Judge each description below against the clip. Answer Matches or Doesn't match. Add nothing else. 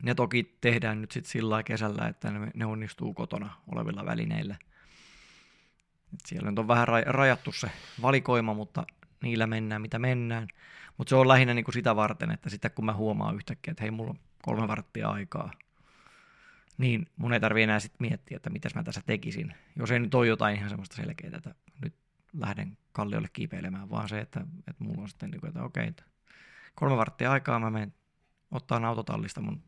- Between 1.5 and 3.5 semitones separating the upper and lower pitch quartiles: Doesn't match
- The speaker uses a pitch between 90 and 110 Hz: Doesn't match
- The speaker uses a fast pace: Matches